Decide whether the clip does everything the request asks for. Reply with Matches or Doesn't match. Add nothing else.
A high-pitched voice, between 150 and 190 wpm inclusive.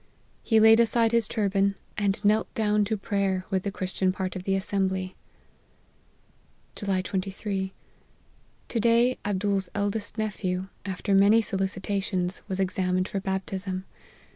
Doesn't match